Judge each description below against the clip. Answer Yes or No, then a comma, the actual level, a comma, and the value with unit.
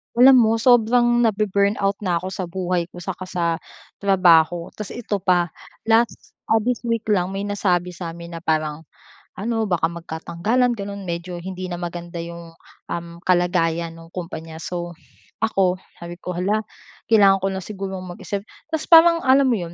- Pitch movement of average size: Yes, average, 3.8 semitones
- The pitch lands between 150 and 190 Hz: Yes, medium, 185 Hz